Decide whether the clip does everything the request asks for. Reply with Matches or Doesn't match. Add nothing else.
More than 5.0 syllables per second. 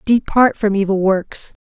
Doesn't match